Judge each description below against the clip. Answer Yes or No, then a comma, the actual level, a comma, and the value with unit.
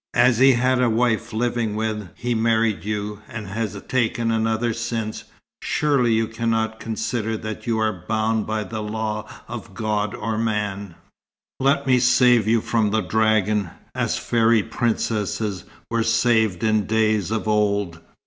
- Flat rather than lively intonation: Yes, narrow, 1.5 semitones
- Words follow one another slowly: No, average, 150 wpm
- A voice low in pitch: Yes, low, 110 Hz